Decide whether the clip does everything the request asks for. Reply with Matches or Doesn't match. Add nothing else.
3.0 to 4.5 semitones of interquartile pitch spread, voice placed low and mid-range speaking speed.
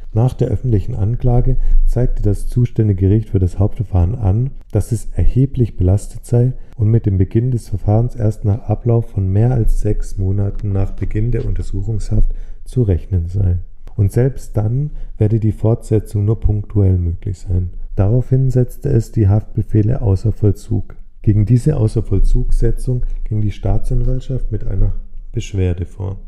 Matches